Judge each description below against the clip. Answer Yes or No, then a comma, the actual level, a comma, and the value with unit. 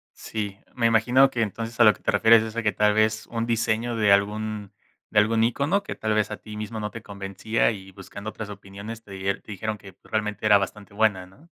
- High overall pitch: No, low, 110 Hz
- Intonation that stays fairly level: Yes, narrow, 1.9 semitones